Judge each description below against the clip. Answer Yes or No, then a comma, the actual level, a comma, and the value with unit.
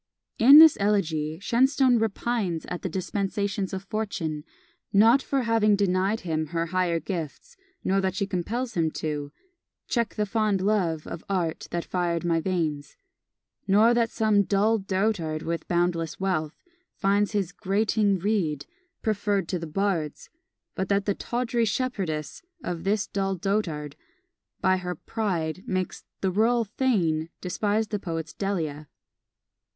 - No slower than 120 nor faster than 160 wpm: Yes, average, 140 wpm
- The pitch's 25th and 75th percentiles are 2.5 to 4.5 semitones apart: Yes, average, 4.1 semitones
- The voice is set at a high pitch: Yes, high, 195 Hz